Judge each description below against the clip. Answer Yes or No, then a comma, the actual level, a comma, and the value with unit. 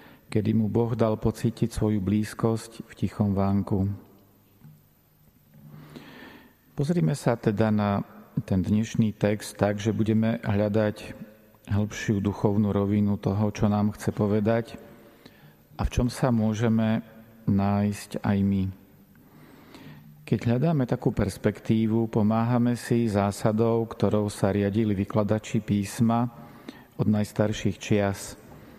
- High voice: No, low, 110 Hz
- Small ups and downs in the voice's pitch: Yes, narrow, 2.1 semitones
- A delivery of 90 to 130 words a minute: Yes, slow, 110 wpm